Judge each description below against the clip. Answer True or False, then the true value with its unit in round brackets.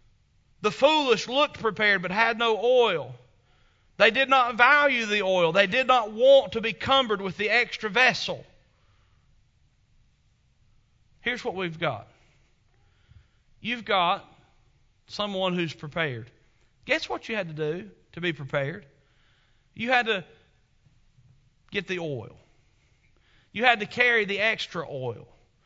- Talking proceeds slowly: True (130 wpm)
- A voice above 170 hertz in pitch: True (185 Hz)